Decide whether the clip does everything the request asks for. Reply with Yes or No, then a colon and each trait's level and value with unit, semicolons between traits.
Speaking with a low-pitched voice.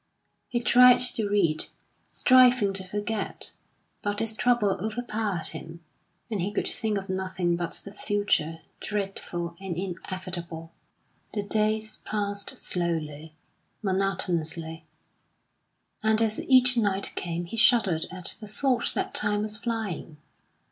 No: high, 200 Hz